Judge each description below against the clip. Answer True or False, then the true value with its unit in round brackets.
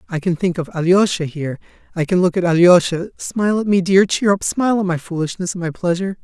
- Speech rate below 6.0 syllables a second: False (6.2 syllables/s)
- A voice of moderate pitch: True (180 Hz)